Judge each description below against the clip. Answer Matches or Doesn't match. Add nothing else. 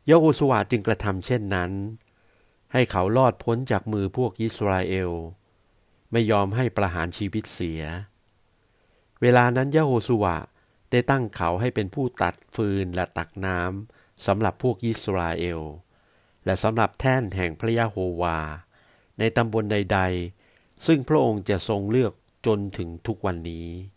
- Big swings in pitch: Doesn't match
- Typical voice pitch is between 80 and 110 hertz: Matches